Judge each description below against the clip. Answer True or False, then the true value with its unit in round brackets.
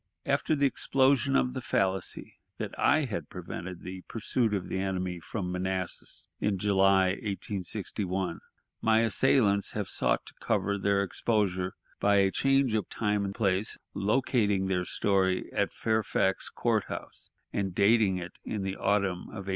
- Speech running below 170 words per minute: True (155 wpm)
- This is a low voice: True (100 Hz)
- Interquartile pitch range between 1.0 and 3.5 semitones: True (2.8 semitones)